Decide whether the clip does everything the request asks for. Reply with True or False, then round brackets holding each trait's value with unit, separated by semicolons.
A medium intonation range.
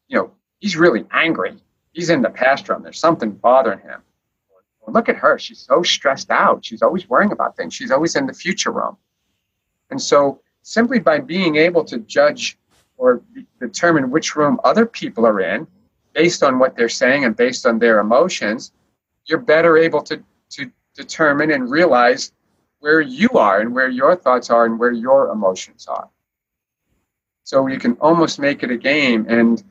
False (6.3 semitones)